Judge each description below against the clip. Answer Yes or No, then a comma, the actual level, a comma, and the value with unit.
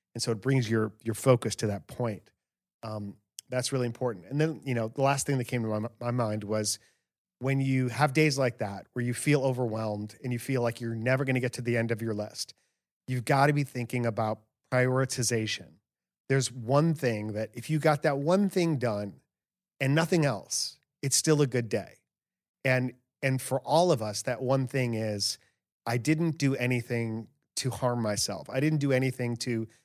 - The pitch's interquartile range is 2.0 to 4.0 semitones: Yes, average, 3.3 semitones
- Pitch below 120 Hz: No, low, 125 Hz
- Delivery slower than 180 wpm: No, fast, 205 wpm